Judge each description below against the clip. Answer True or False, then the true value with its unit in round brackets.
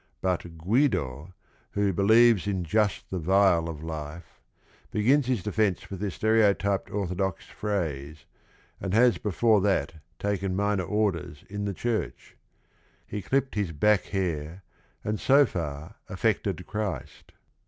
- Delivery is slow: True (130 wpm)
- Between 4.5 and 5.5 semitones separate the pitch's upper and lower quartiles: False (3.7 semitones)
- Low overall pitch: True (100 Hz)